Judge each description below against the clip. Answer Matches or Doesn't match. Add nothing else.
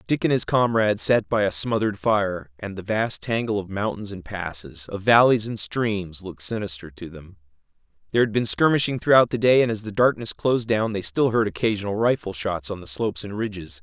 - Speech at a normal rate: Doesn't match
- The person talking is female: Doesn't match